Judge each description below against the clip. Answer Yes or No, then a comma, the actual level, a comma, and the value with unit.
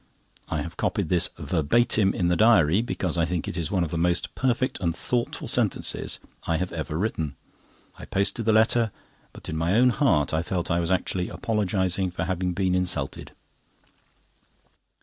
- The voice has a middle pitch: No, very low, 90 Hz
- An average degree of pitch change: Yes, average, 4.2 semitones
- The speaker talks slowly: No, average, 175 wpm